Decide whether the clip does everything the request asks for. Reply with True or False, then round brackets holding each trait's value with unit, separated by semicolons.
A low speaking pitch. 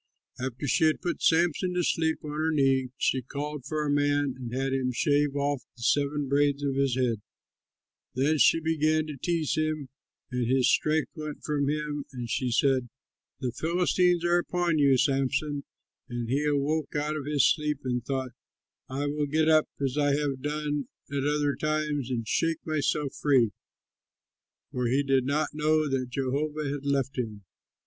False (145 Hz)